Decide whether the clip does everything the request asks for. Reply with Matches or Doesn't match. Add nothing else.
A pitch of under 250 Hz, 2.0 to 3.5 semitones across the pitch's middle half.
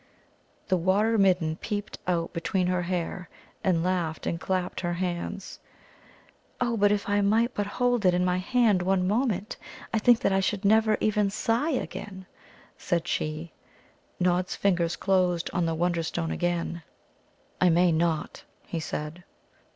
Matches